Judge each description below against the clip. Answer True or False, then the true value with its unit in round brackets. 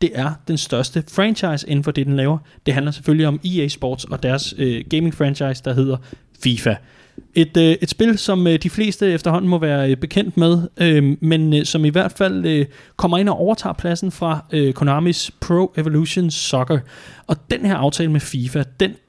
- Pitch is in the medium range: True (155 Hz)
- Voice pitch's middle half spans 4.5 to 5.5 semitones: False (3.8 semitones)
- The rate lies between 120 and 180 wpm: True (175 wpm)